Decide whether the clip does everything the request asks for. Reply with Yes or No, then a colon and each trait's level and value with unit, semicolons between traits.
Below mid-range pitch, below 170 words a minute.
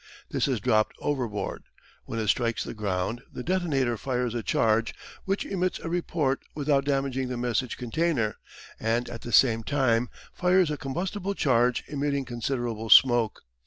Yes: low, 125 Hz; average, 155 wpm